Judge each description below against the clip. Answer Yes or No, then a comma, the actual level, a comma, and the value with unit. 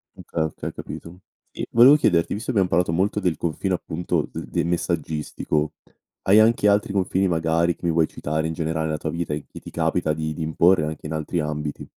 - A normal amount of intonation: Yes, average, 3.0 semitones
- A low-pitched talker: Yes, very low, 85 Hz